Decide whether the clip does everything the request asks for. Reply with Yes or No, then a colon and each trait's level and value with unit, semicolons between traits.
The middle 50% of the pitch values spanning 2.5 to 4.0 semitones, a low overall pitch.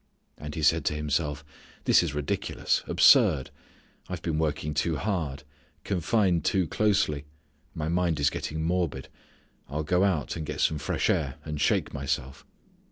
Yes: average, 3.0 semitones; very low, 80 Hz